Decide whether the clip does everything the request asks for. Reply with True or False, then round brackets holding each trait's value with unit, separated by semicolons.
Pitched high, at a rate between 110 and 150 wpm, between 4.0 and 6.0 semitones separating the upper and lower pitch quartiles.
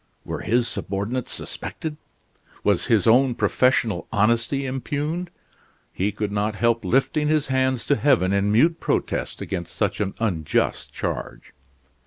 False (115 Hz; 135 wpm; 4.7 semitones)